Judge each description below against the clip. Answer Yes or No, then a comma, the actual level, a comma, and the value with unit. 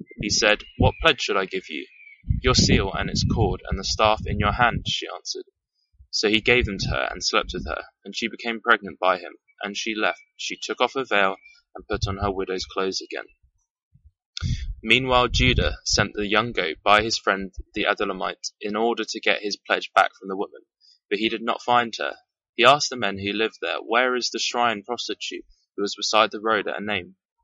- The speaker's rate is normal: No, fast, 215 wpm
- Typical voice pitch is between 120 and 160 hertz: No, low, 110 Hz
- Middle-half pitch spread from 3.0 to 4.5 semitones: Yes, average, 3.9 semitones